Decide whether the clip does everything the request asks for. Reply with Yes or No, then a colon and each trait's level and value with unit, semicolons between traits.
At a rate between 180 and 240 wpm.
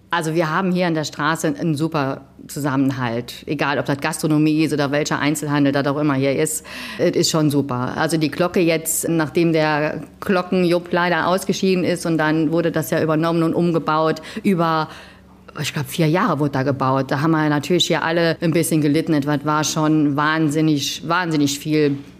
Yes: average, 185 wpm